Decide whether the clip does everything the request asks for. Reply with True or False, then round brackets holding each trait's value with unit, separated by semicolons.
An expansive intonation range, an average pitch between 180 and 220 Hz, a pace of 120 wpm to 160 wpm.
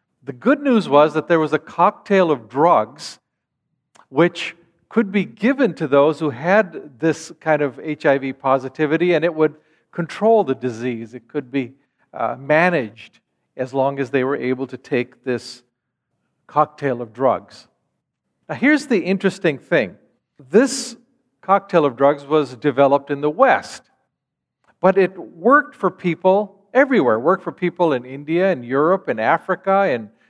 False (5.8 semitones; 155 Hz; 155 wpm)